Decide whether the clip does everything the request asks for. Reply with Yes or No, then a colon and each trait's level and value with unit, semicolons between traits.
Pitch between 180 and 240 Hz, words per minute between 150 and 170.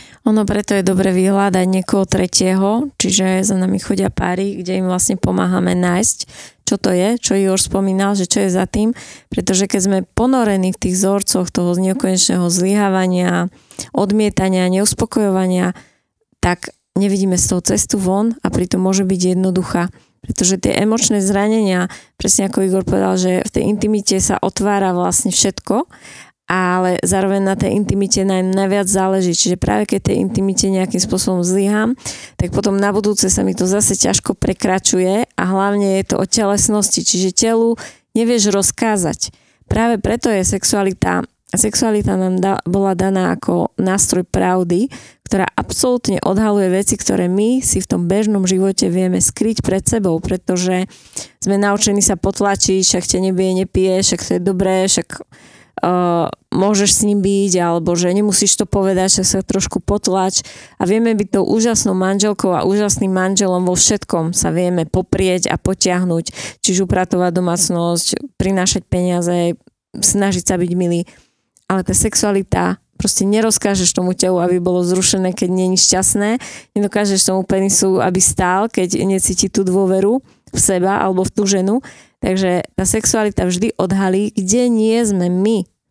Yes: high, 190 Hz; average, 155 wpm